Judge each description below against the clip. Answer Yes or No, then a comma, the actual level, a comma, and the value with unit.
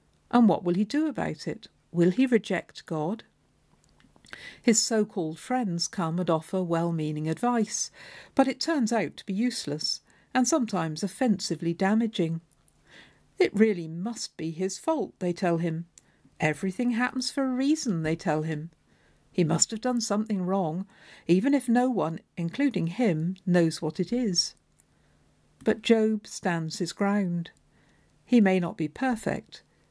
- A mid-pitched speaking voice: No, high, 195 Hz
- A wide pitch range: Yes, wide, 5.9 semitones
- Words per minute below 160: Yes, average, 150 wpm